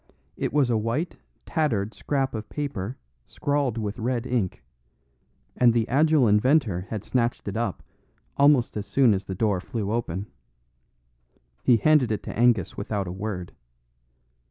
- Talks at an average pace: Yes, average, 150 wpm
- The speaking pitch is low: Yes, low, 115 Hz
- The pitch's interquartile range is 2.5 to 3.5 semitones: No, average, 4.4 semitones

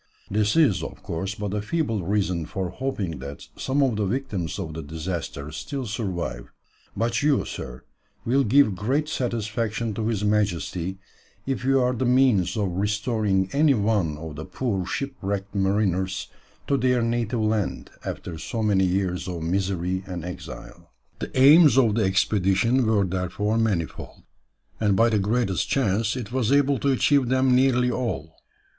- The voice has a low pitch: Yes, low, 105 Hz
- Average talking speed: Yes, average, 160 wpm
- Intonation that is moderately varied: Yes, average, 5.0 semitones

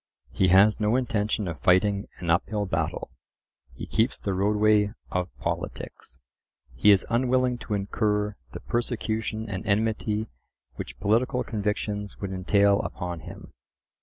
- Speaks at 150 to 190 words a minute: No, slow, 135 wpm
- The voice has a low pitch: Yes, low, 105 Hz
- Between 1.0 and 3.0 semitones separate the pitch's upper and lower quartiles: Yes, narrow, 2.4 semitones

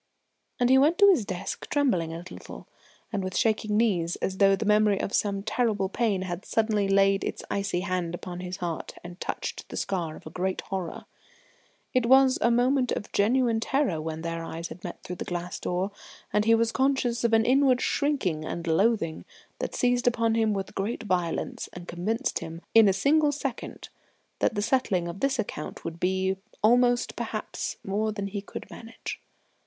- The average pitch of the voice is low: No, high, 200 Hz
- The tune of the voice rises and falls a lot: No, average, 4.7 semitones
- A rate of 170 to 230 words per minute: Yes, average, 190 wpm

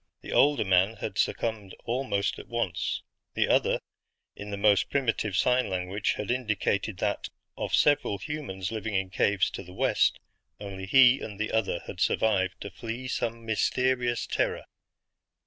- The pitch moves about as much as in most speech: Yes, average, 3.7 semitones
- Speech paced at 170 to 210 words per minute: No, average, 155 wpm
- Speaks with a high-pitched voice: No, low, 105 Hz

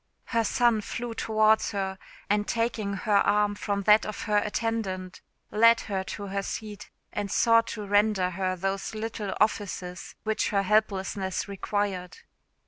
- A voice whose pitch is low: No, high, 205 Hz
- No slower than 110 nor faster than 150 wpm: Yes, average, 145 wpm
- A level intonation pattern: Yes, narrow, 2.0 semitones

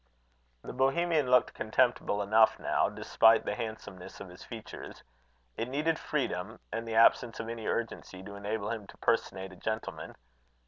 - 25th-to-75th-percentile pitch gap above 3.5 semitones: No, average, 3.2 semitones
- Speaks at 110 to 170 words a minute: Yes, average, 155 wpm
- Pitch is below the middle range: Yes, low, 110 Hz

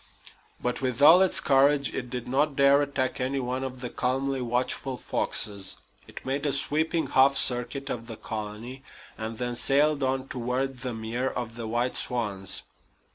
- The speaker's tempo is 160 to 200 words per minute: Yes, average, 170 wpm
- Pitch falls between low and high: No, low, 130 Hz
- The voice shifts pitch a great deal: No, narrow, 2.4 semitones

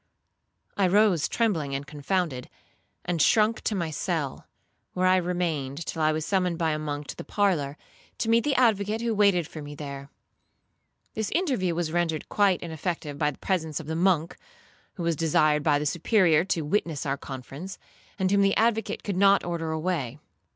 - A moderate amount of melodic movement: Yes, average, 4.6 semitones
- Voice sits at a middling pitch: Yes, medium, 170 Hz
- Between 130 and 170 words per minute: No, average, 180 wpm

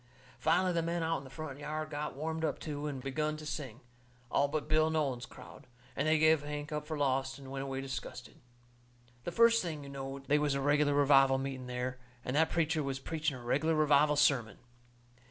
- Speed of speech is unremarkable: No, fast, 210 wpm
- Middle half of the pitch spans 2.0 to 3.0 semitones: Yes, narrow, 2.5 semitones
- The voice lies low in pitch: No, medium, 145 Hz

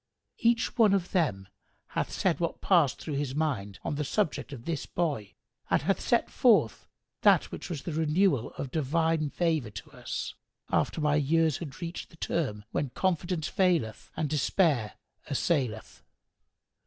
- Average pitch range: Yes, average, 3.9 semitones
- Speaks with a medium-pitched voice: Yes, medium, 155 Hz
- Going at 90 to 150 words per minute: No, average, 160 wpm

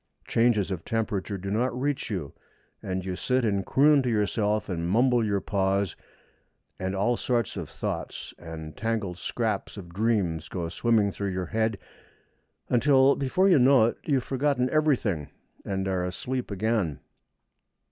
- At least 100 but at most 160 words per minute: Yes, average, 155 wpm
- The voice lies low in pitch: Yes, low, 105 Hz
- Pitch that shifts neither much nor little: Yes, average, 4.8 semitones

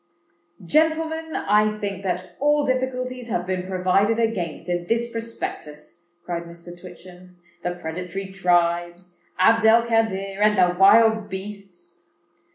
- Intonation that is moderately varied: Yes, average, 4.3 semitones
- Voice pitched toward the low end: No, high, 190 Hz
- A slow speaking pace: Yes, slow, 120 wpm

